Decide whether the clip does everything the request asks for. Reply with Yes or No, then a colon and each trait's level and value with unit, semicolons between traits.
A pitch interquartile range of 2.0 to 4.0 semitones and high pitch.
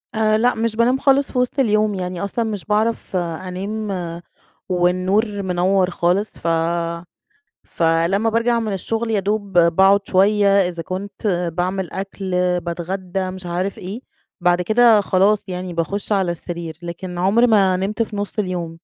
Yes: average, 3.1 semitones; high, 195 Hz